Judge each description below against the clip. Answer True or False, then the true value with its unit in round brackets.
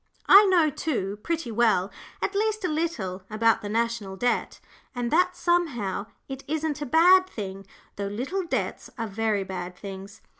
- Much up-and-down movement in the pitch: True (8.7 semitones)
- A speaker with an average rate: True (160 wpm)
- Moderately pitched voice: False (235 Hz)